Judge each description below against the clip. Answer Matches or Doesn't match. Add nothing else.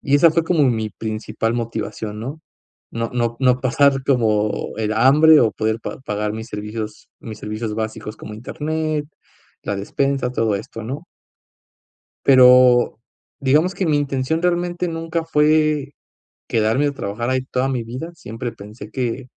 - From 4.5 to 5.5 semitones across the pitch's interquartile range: Matches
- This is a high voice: Doesn't match